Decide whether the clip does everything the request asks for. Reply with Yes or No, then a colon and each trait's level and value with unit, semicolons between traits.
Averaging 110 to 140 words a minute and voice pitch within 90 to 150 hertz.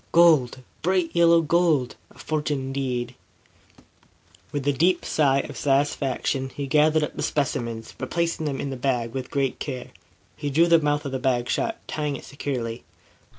No: average, 165 wpm; medium, 140 Hz